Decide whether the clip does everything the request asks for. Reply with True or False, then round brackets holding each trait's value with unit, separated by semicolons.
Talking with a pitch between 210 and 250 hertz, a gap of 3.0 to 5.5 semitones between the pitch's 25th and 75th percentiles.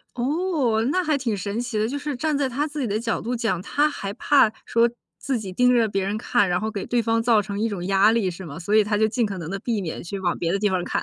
True (220 Hz; 4.0 semitones)